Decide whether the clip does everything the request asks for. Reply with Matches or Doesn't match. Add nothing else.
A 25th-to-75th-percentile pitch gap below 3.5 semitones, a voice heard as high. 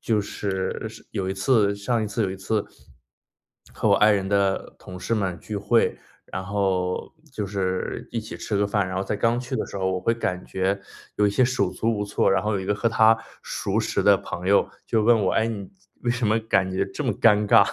Doesn't match